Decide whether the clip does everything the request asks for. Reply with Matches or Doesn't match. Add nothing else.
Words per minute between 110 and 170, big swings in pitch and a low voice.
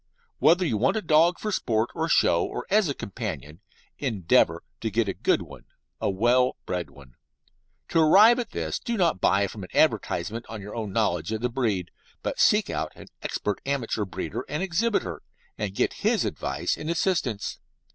Doesn't match